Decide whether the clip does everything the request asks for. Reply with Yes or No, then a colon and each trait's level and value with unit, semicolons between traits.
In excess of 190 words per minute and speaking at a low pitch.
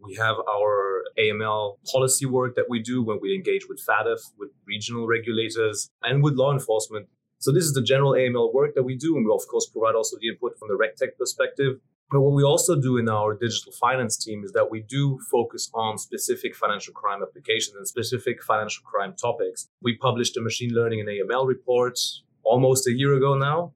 Yes: fast, 205 wpm; low, 130 Hz